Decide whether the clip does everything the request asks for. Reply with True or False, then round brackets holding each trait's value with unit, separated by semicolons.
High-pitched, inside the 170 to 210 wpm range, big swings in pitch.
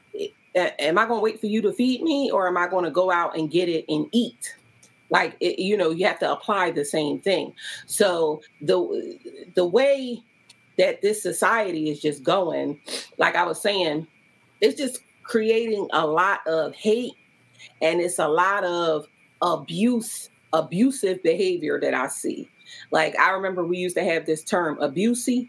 True (195 Hz; 180 wpm; 6.8 semitones)